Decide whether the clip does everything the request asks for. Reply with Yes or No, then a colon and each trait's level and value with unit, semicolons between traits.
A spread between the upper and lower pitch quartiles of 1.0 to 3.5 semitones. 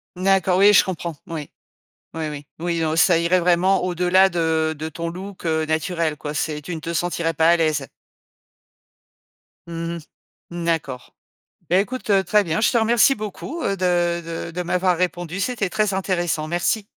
Yes: average, 2.7 semitones